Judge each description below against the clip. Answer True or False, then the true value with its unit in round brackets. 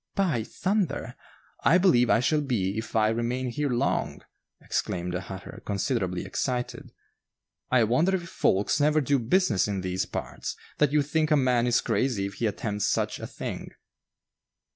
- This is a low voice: True (125 Hz)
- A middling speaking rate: True (165 wpm)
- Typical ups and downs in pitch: False (6.3 semitones)